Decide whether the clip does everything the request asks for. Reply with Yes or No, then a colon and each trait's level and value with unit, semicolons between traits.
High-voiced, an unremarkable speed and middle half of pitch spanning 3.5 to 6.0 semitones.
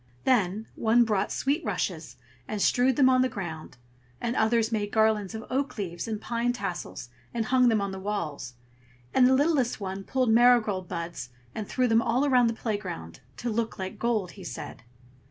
Yes: high, 220 Hz; average, 185 wpm; average, 4.2 semitones